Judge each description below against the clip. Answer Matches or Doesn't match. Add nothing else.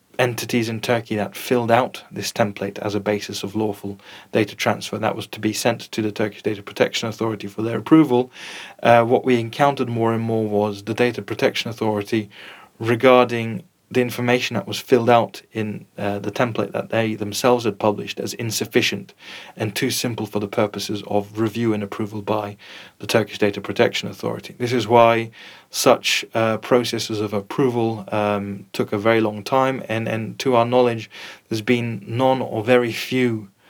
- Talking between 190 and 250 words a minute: Doesn't match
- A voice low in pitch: Matches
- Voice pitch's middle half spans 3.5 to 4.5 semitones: Doesn't match